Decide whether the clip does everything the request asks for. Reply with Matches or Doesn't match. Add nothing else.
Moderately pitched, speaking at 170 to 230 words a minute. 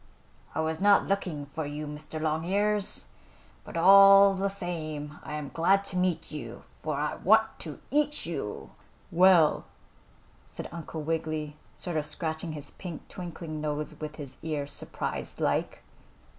Doesn't match